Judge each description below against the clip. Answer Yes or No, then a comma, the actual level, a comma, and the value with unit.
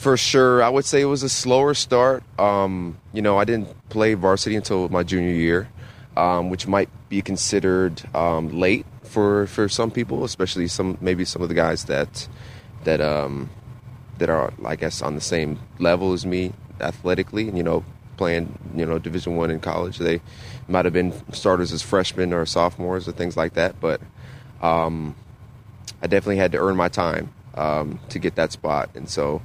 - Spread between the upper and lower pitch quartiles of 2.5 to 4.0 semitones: No, average, 4.5 semitones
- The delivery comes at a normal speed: Yes, average, 185 wpm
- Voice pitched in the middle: No, very low, 95 Hz